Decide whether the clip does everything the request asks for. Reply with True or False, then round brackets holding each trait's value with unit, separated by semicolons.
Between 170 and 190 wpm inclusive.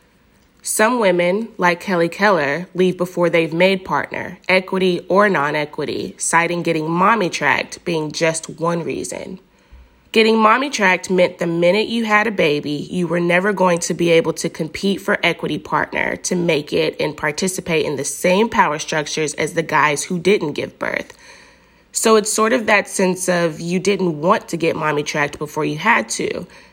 True (175 wpm)